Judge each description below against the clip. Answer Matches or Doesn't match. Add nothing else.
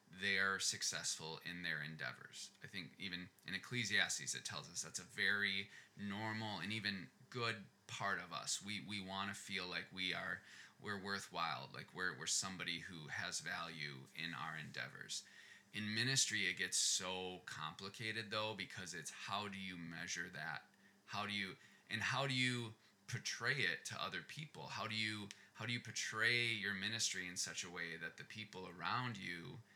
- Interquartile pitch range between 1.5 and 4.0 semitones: Matches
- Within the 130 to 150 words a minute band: Doesn't match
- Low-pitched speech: Matches